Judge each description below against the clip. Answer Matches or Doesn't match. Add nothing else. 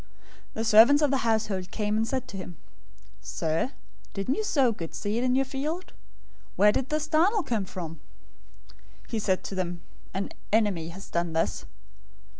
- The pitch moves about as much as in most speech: Doesn't match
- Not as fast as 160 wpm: Doesn't match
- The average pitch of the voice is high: Matches